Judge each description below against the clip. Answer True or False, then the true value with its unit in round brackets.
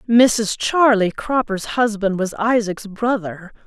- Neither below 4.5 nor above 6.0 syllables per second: False (3.6 syllables/s)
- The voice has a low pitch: False (215 Hz)